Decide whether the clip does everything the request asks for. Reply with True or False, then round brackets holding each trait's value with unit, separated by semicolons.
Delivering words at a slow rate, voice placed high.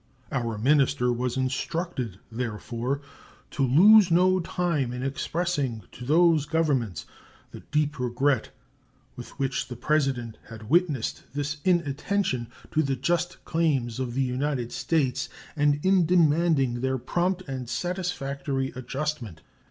False (125 wpm; 140 Hz)